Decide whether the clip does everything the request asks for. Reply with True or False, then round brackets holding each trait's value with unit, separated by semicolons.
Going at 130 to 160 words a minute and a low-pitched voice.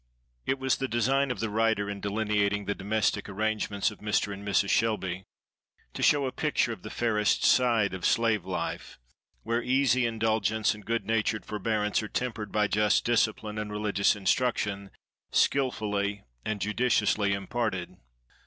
True (155 wpm; 110 Hz)